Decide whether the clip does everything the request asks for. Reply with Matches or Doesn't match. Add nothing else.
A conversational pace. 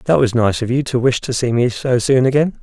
Doesn't match